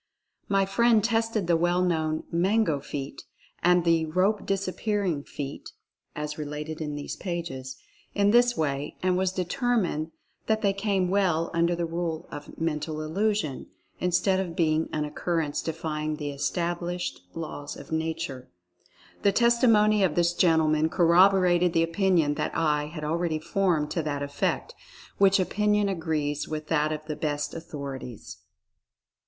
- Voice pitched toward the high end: No, medium, 165 Hz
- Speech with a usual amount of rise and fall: Yes, average, 4.0 semitones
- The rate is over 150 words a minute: No, average, 145 wpm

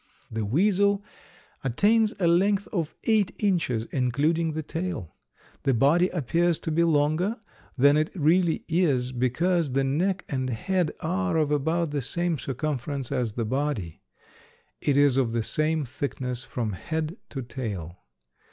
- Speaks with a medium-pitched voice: Yes, medium, 150 Hz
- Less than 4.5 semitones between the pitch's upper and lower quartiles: No, average, 5.2 semitones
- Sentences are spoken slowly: No, average, 145 wpm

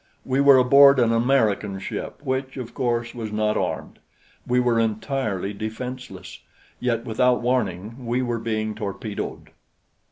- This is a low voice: Yes, low, 120 Hz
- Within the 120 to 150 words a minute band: Yes, slow, 135 wpm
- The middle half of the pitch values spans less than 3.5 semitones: Yes, average, 2.8 semitones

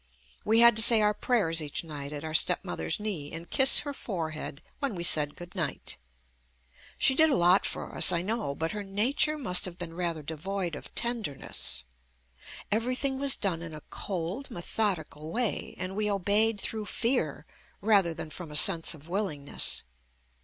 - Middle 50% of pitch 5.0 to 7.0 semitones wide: Yes, wide, 5.4 semitones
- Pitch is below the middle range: No, medium, 185 Hz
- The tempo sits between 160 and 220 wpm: Yes, average, 175 wpm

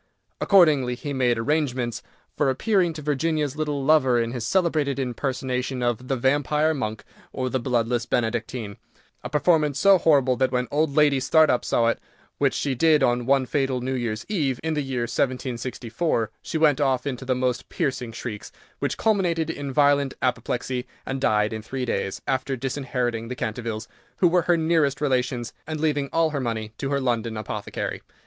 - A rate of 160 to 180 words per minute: Yes, average, 175 wpm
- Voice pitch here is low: Yes, low, 130 Hz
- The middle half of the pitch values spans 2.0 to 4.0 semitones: Yes, average, 3.5 semitones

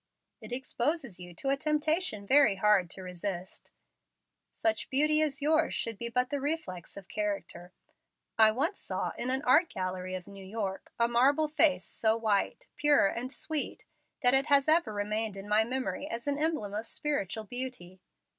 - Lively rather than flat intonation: Yes, wide, 6.3 semitones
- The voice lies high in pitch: Yes, high, 235 Hz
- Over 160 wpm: Yes, average, 175 wpm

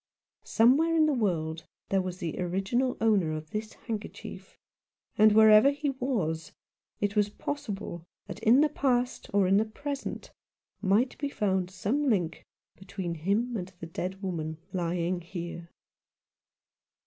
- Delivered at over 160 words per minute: No, average, 140 wpm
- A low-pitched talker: No, high, 205 Hz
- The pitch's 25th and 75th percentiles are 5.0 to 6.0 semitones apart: Yes, wide, 5.6 semitones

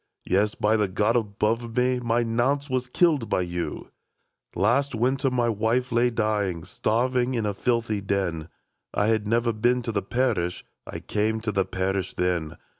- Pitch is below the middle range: Yes, low, 115 Hz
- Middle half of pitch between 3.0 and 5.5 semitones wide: Yes, average, 3.4 semitones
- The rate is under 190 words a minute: Yes, average, 180 wpm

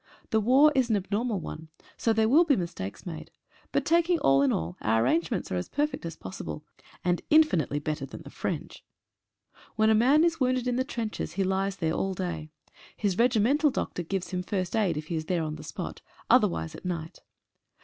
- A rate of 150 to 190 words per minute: No, average, 200 wpm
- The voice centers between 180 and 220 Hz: Yes, high, 190 Hz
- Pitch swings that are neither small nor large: No, wide, 7.6 semitones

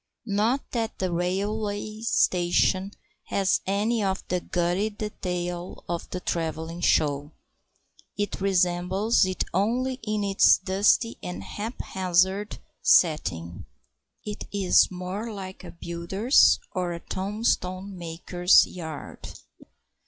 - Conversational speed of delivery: No, slow, 110 wpm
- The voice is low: No, medium, 185 Hz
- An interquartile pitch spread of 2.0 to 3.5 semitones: Yes, average, 2.9 semitones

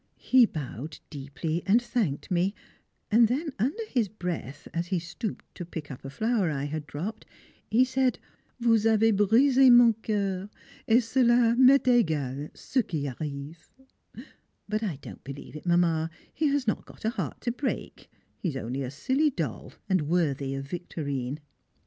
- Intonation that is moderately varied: No, wide, 8.2 semitones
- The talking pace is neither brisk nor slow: Yes, average, 165 wpm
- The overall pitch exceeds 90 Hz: Yes, high, 190 Hz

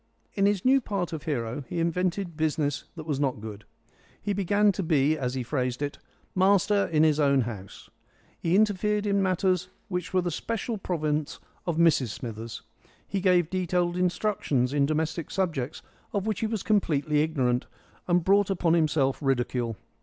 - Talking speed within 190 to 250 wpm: No, average, 170 wpm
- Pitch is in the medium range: Yes, medium, 165 Hz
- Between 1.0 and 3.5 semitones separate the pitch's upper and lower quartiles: No, average, 5.1 semitones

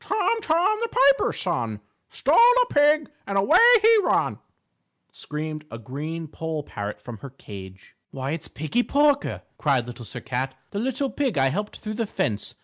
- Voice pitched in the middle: Yes, medium, 165 Hz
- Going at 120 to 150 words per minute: No, average, 170 wpm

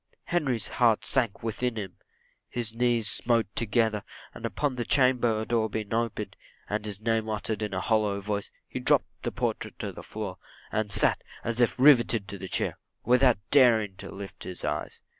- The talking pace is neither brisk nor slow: Yes, average, 180 wpm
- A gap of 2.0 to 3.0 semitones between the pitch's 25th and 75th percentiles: Yes, narrow, 2.6 semitones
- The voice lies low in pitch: Yes, low, 110 Hz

